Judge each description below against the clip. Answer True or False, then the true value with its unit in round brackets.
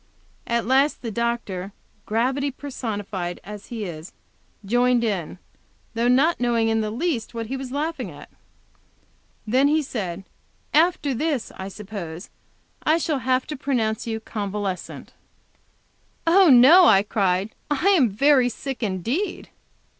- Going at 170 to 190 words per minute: False (135 wpm)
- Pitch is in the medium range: False (235 Hz)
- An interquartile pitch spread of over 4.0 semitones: True (5.1 semitones)